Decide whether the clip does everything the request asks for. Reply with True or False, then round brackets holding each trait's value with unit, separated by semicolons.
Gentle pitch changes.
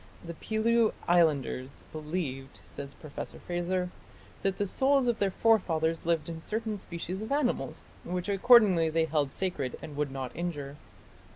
False (5.1 semitones)